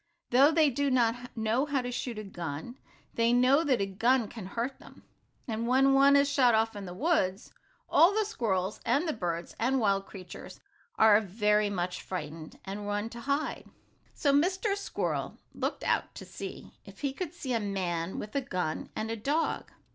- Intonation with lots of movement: Yes, wide, 5.7 semitones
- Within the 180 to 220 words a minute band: Yes, average, 190 wpm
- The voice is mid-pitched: No, high, 230 Hz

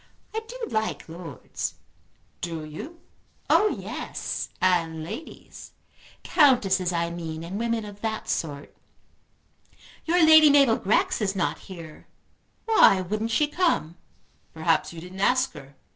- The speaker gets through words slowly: Yes, slow, 130 wpm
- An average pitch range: No, wide, 7.8 semitones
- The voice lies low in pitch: No, high, 195 Hz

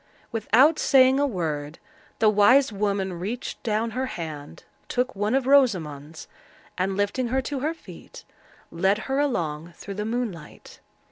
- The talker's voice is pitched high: Yes, high, 210 Hz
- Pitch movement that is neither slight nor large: No, wide, 6.5 semitones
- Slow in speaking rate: No, average, 145 wpm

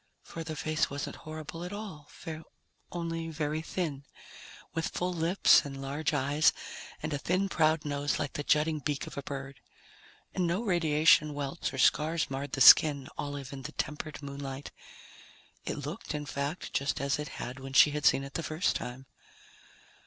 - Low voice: No, medium, 150 Hz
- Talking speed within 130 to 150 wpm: No, average, 175 wpm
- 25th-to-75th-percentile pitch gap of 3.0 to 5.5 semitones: No, narrow, 2.5 semitones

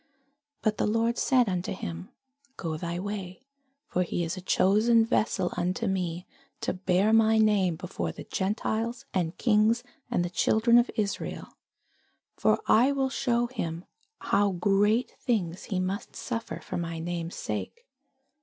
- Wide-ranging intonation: No, average, 4.3 semitones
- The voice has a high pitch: Yes, high, 200 Hz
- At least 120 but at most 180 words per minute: Yes, average, 150 wpm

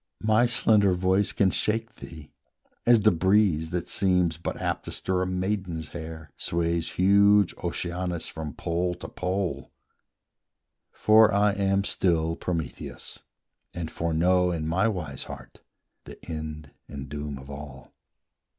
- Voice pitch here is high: No, very low, 90 Hz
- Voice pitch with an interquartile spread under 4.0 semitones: Yes, average, 3.5 semitones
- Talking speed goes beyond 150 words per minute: No, slow, 135 wpm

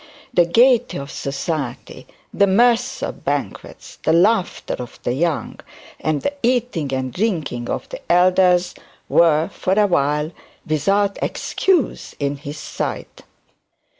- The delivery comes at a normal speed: No, slow, 125 wpm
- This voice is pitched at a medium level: Yes, medium, 170 Hz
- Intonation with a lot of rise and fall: Yes, wide, 5.9 semitones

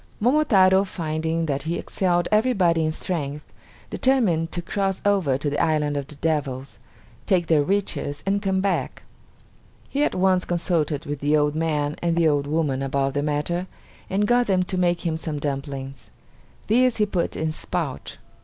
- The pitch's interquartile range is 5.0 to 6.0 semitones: No, average, 4.4 semitones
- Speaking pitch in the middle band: Yes, medium, 165 Hz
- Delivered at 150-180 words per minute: Yes, average, 175 wpm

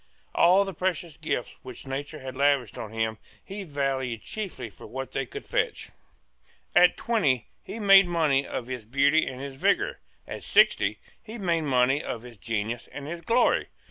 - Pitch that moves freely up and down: Yes, wide, 5.7 semitones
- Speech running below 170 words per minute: No, average, 175 wpm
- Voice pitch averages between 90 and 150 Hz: Yes, medium, 140 Hz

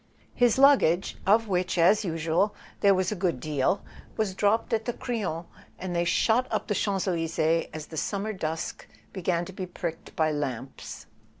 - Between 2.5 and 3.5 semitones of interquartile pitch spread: No, average, 4.0 semitones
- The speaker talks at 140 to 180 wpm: Yes, average, 175 wpm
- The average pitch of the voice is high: No, medium, 180 Hz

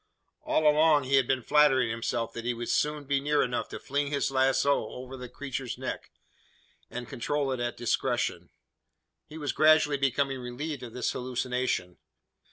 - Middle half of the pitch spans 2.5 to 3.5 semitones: Yes, average, 2.9 semitones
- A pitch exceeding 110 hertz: Yes, low, 135 Hz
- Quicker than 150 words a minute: Yes, average, 170 wpm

